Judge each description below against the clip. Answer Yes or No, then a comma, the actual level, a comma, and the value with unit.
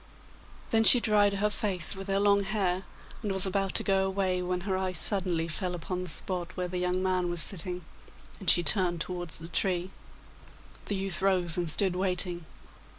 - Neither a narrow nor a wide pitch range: No, narrow, 1.7 semitones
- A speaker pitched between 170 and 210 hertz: Yes, medium, 185 Hz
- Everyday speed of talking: Yes, average, 190 wpm